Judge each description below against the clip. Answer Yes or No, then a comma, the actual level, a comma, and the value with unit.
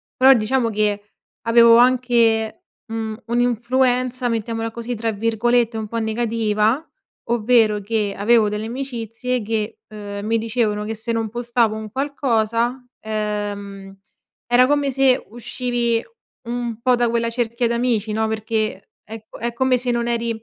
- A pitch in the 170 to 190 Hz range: No, high, 230 Hz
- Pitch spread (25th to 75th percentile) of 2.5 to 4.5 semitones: No, narrow, 1.9 semitones